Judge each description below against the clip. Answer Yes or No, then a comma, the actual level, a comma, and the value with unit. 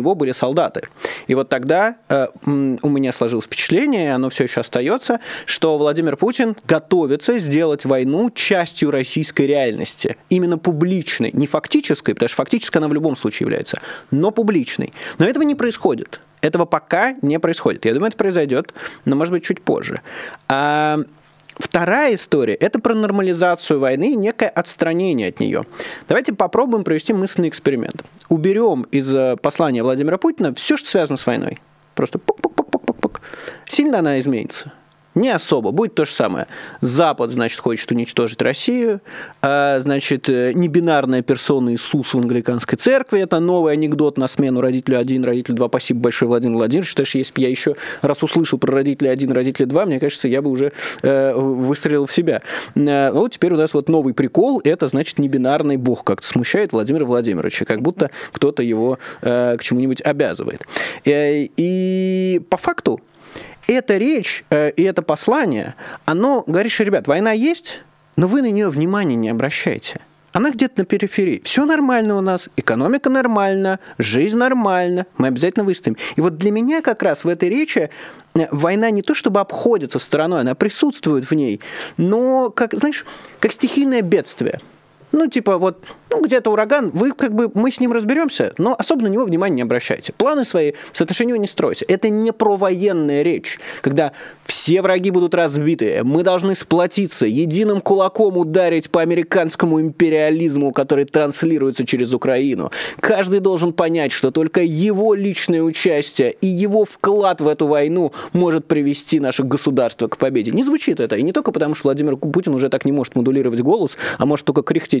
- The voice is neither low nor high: Yes, medium, 165 Hz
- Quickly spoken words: Yes, fast, 165 wpm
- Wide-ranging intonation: Yes, wide, 6.7 semitones